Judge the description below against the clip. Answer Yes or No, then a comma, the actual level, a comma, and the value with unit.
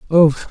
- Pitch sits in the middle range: Yes, medium, 160 Hz